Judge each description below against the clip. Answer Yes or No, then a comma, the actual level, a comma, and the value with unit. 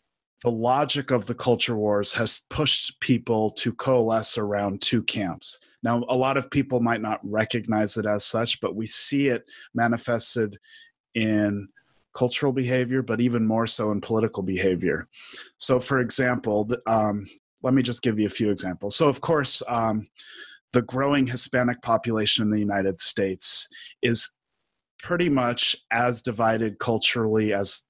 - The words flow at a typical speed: Yes, average, 155 wpm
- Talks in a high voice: No, low, 115 Hz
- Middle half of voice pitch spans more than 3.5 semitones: No, average, 2.8 semitones